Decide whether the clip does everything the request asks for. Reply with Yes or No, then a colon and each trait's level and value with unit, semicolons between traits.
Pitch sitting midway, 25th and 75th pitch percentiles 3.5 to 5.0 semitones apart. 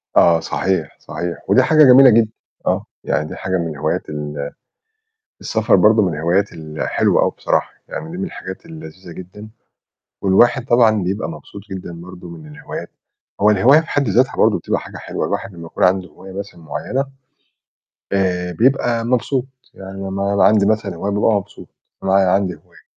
No: very low, 95 Hz; average, 4.1 semitones